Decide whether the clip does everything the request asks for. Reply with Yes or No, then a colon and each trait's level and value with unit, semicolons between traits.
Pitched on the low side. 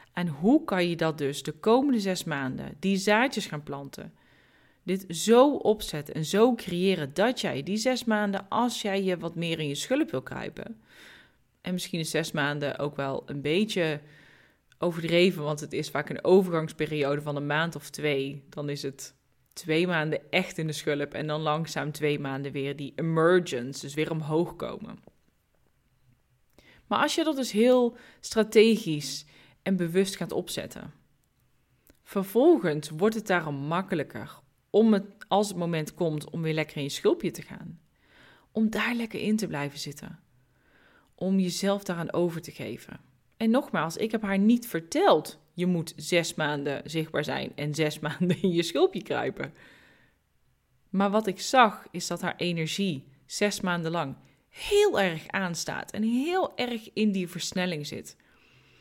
No: medium, 175 Hz